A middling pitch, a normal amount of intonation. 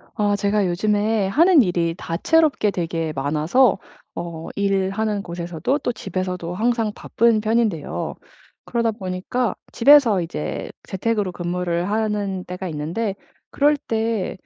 No: high, 200 Hz; average, 4.3 semitones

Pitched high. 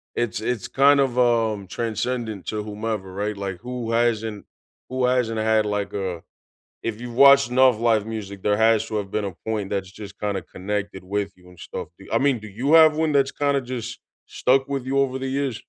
No: low, 110 Hz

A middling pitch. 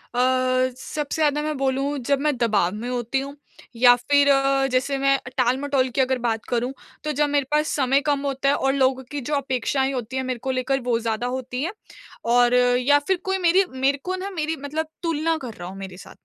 No: very high, 270 Hz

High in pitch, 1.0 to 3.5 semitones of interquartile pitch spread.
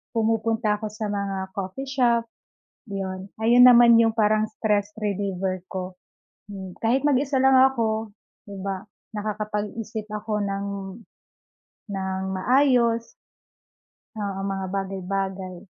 Yes: high, 210 Hz; average, 2.9 semitones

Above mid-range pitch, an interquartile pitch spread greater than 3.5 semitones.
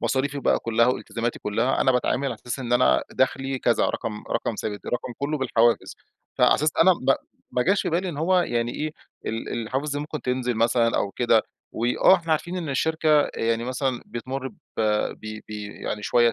No: low, 125 Hz; average, 3.9 semitones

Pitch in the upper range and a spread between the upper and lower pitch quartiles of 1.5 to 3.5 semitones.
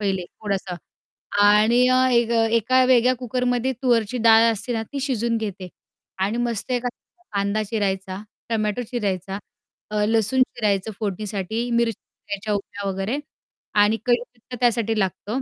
Yes: high, 220 Hz; average, 3.1 semitones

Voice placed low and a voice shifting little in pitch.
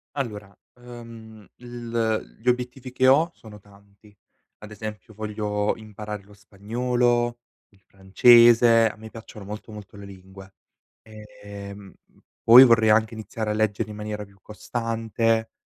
Yes: low, 110 Hz; narrow, 2.2 semitones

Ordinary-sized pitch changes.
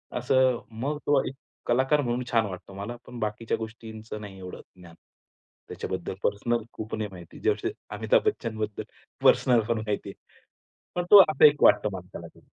Yes: average, 4.1 semitones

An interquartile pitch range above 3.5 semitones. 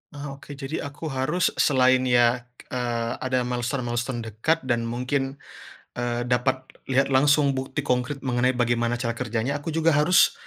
No: average, 2.7 semitones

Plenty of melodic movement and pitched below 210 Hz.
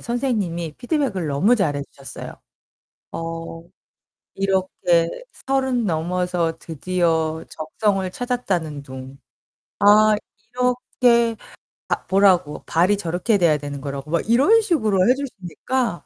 Yes: wide, 6.4 semitones; medium, 185 Hz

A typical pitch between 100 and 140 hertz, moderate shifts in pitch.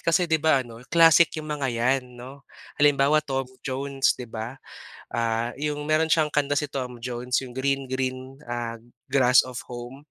Yes: low, 135 Hz; average, 3.0 semitones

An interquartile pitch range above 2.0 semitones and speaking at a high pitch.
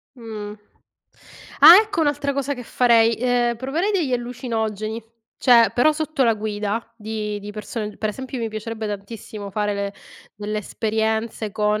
Yes: average, 2.8 semitones; high, 225 Hz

